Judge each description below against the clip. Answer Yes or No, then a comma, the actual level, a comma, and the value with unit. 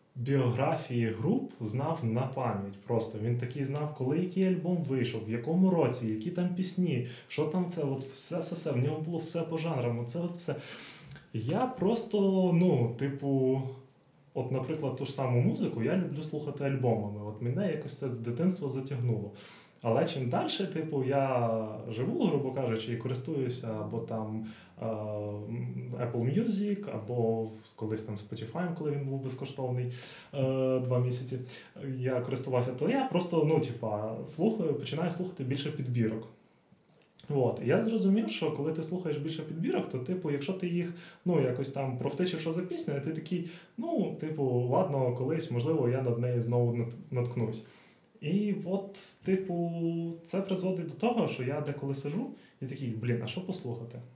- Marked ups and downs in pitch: Yes, wide, 5.7 semitones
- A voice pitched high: No, medium, 140 Hz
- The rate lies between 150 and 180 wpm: Yes, fast, 155 wpm